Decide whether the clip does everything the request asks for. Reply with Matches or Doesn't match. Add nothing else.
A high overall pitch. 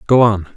Doesn't match